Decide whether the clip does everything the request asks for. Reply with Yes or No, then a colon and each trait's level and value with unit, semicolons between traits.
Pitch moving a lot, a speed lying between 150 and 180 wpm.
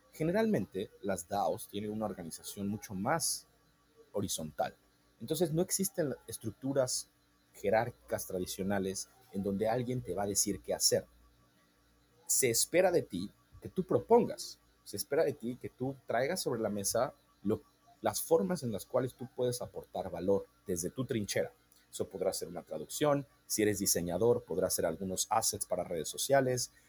Yes: wide, 6.7 semitones; average, 155 wpm